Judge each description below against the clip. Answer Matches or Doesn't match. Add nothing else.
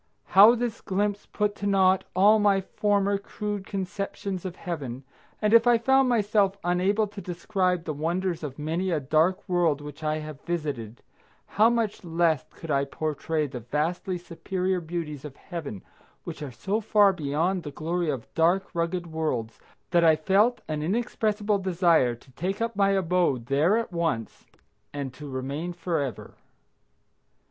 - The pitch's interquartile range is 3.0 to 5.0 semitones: Matches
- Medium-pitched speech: Matches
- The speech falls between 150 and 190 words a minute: Matches